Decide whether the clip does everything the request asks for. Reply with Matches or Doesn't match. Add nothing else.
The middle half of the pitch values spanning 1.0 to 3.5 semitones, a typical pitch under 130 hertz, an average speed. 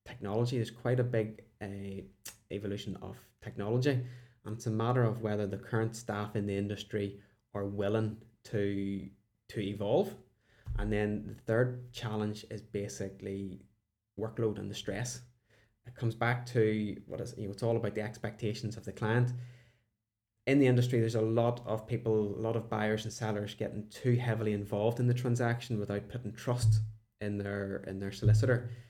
Matches